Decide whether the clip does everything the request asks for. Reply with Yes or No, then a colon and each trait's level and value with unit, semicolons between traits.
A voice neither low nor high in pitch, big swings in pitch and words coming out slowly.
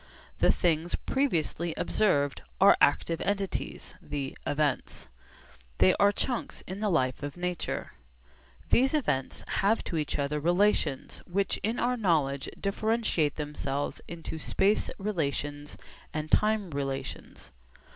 Yes: medium, 165 Hz; wide, 5.9 semitones; slow, 120 wpm